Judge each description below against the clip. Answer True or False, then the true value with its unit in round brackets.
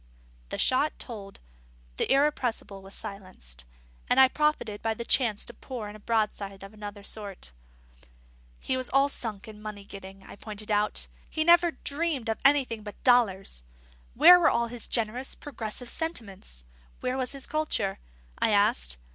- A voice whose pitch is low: False (220 Hz)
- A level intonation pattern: False (4.5 semitones)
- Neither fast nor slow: True (160 wpm)